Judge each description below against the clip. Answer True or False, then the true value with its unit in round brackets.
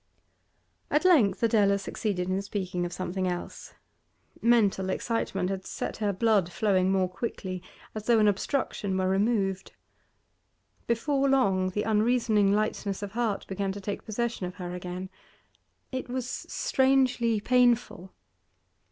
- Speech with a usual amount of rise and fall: True (3.8 semitones)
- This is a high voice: True (205 Hz)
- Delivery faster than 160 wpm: False (135 wpm)